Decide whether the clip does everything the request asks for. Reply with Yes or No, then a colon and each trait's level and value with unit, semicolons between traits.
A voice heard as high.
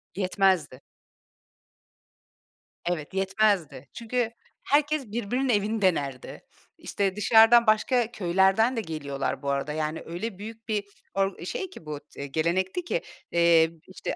Yes: high, 195 Hz